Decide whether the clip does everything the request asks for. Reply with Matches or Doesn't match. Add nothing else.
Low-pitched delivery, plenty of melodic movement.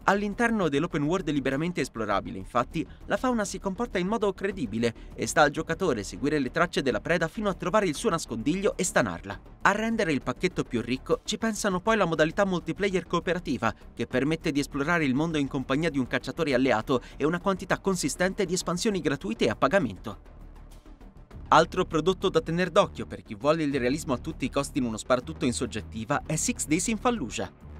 Doesn't match